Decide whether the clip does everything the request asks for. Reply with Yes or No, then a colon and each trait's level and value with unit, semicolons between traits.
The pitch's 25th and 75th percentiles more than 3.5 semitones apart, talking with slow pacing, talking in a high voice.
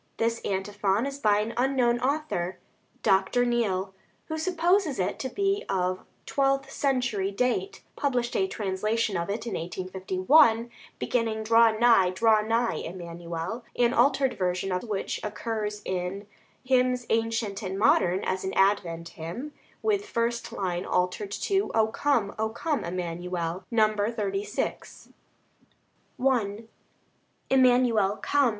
Yes: average, 4.7 semitones; slow, 130 wpm; high, 220 Hz